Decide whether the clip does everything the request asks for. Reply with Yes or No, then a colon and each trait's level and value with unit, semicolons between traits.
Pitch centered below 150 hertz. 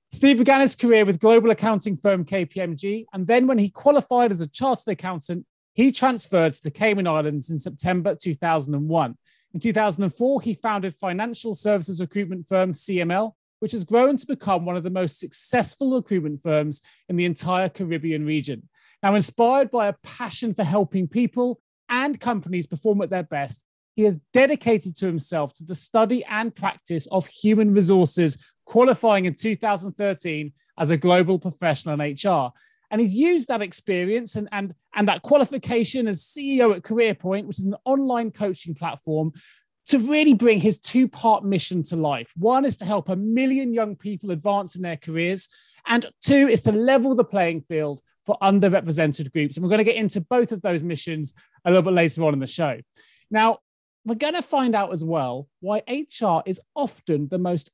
No: high, 195 Hz